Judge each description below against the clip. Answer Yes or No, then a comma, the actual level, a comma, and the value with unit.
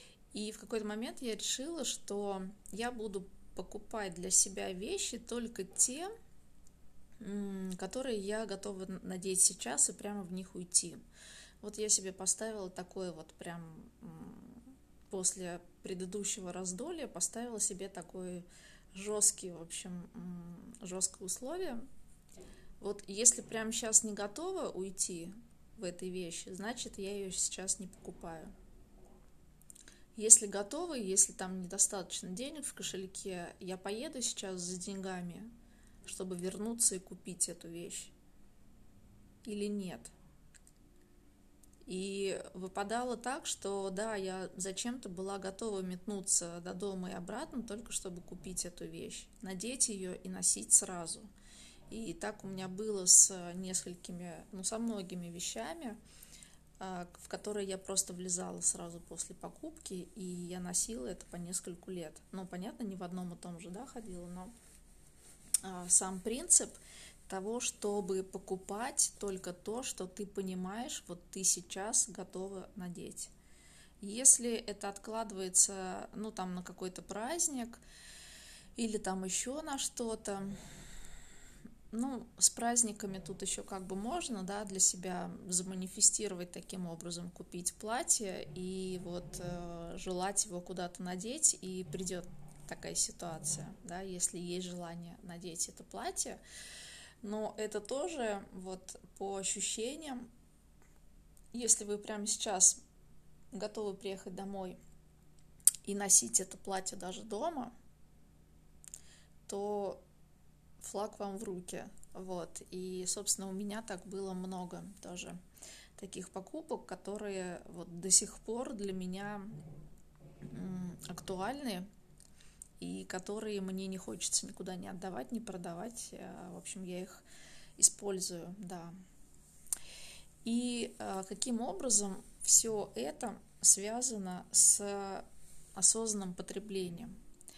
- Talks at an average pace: Yes, average, 120 wpm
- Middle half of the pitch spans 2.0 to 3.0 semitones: Yes, average, 2.7 semitones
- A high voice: Yes, high, 195 Hz